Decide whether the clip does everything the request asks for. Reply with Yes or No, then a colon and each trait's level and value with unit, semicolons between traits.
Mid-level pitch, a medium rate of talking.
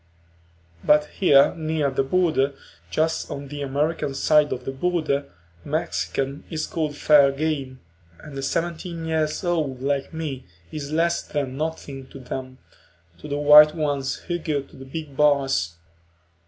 Yes: medium, 145 Hz; average, 155 wpm